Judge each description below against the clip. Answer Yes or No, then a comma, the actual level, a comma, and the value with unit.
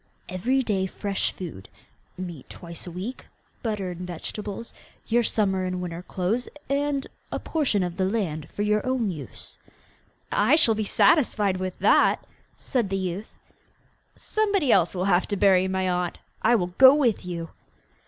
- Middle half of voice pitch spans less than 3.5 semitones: No, average, 4.4 semitones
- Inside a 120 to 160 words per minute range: Yes, average, 155 wpm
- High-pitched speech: Yes, high, 195 Hz